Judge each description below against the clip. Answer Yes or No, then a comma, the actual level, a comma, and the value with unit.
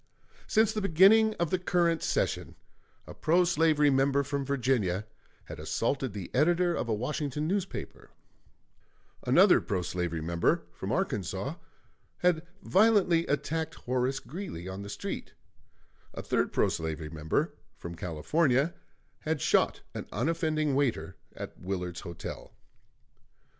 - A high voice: No, medium, 140 Hz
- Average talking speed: No, slow, 125 wpm